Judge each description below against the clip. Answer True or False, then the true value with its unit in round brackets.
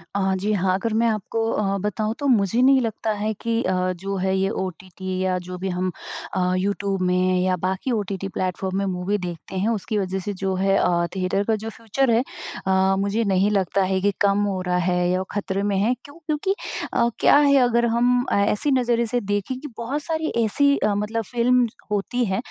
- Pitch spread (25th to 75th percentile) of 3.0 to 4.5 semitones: True (3.6 semitones)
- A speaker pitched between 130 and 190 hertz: False (200 Hz)